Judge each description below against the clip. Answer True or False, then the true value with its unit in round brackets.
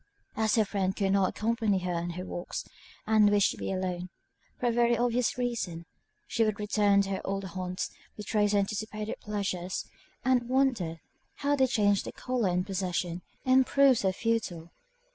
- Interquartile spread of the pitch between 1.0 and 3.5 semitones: False (3.9 semitones)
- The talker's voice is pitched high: True (205 Hz)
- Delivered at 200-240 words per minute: False (175 wpm)